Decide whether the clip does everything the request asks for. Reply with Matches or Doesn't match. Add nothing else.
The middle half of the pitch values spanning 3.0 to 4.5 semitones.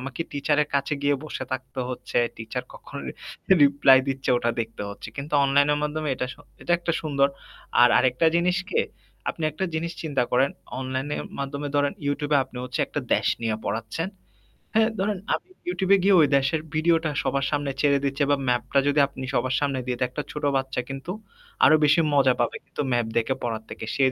Doesn't match